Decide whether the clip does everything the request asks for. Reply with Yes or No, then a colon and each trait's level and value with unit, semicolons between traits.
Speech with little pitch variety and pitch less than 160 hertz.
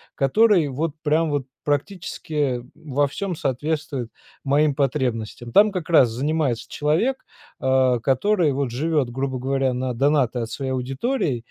No: average, 3.5 semitones; medium, 140 Hz